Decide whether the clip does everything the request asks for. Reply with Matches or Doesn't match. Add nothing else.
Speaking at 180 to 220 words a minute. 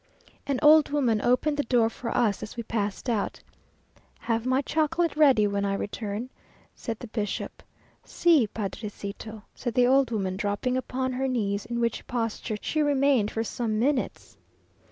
Doesn't match